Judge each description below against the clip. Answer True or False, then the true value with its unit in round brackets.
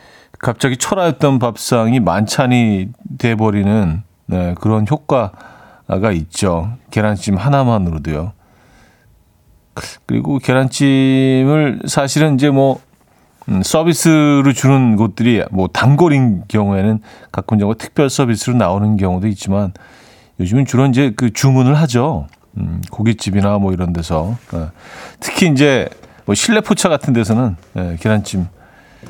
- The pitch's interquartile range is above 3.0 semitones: True (5.5 semitones)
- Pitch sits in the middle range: False (110 Hz)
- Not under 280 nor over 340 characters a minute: False (265 characters per minute)